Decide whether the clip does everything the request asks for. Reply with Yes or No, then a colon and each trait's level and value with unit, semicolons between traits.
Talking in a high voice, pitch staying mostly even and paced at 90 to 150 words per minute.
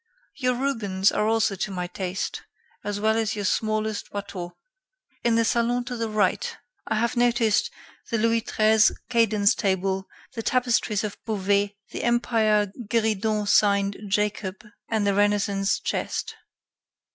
Yes: high, 215 Hz; narrow, 2.3 semitones; average, 140 wpm